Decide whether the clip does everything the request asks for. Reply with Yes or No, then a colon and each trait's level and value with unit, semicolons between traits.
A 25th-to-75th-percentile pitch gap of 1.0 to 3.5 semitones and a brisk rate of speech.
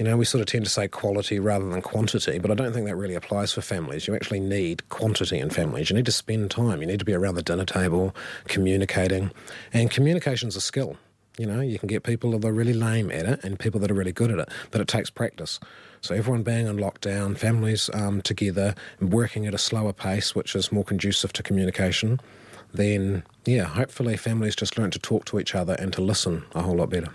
Yes: average, 2.7 semitones; fast, 235 wpm